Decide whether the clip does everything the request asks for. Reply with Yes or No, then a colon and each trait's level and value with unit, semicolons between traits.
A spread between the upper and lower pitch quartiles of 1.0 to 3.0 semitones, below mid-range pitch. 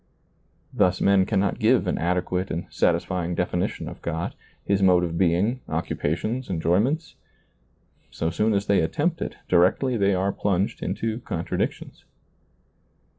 Yes: average, 2.7 semitones; very low, 90 Hz